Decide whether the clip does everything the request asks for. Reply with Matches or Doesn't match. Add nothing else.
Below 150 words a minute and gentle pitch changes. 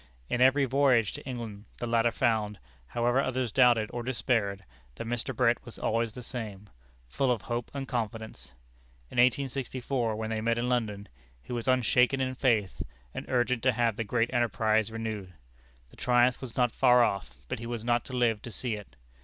Doesn't match